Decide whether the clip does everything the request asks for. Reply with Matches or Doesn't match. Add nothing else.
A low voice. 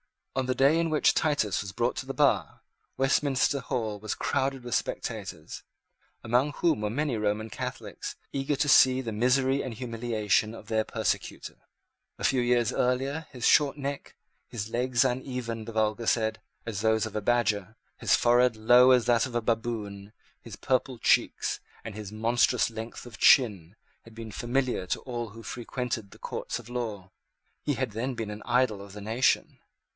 Matches